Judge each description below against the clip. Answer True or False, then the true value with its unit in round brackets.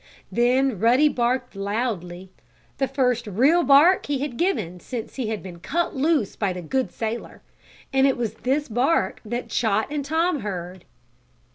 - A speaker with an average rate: True (160 wpm)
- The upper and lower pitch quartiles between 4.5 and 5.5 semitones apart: True (5.0 semitones)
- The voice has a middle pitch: False (245 Hz)